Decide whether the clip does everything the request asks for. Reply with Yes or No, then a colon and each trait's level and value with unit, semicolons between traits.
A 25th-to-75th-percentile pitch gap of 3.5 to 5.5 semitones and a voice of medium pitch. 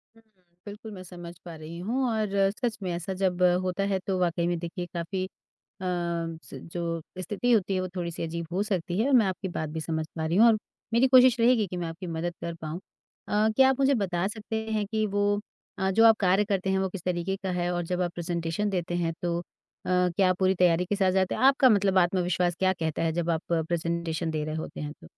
No: average, 3.0 semitones; medium, 180 Hz